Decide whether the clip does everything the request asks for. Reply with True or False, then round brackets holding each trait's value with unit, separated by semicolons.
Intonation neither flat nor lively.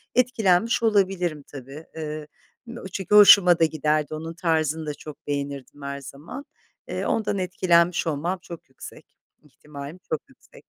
True (4.3 semitones)